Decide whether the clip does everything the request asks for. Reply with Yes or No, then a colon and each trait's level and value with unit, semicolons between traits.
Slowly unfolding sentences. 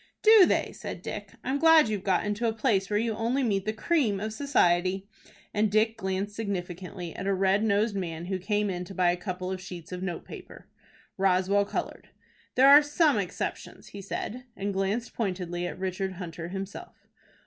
No: average, 185 wpm